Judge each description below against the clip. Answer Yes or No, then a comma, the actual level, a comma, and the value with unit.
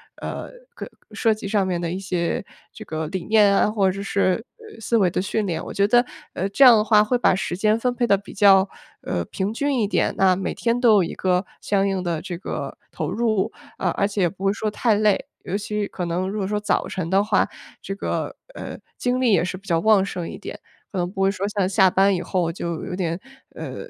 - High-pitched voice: Yes, high, 195 Hz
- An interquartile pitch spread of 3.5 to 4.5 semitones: No, average, 2.7 semitones